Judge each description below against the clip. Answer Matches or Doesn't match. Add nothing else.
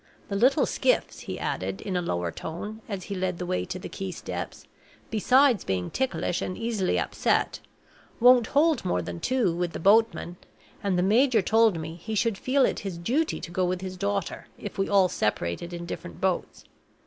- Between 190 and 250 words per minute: Matches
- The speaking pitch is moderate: Doesn't match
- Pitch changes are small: Doesn't match